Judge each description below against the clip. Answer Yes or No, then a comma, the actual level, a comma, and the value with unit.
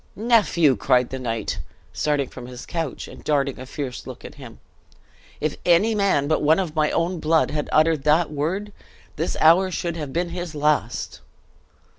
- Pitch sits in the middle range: Yes, medium, 155 Hz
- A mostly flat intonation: No, average, 3.4 semitones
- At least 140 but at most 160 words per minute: No, average, 175 wpm